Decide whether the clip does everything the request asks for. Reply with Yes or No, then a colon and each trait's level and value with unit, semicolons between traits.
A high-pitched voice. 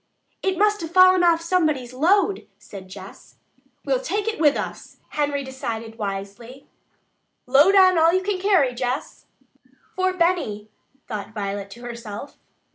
Yes: very high, 290 Hz